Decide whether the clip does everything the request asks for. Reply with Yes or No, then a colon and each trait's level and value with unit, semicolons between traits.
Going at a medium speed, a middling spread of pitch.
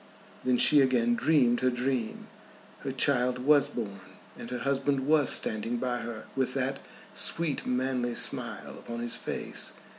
No: average, 150 wpm; narrow, 2.2 semitones